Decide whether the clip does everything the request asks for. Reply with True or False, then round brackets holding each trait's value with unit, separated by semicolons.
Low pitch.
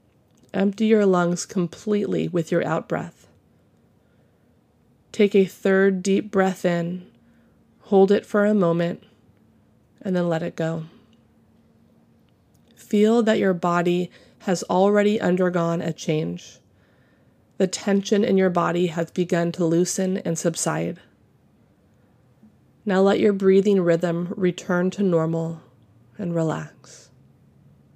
False (180 Hz)